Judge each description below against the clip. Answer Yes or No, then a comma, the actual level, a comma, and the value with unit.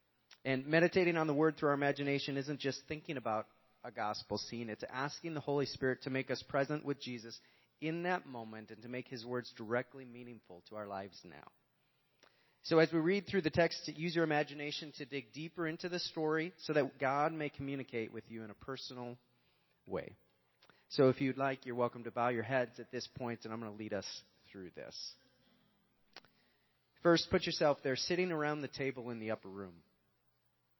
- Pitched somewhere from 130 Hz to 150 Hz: Yes, low, 135 Hz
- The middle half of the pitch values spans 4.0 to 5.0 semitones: Yes, average, 4.6 semitones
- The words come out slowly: No, average, 195 wpm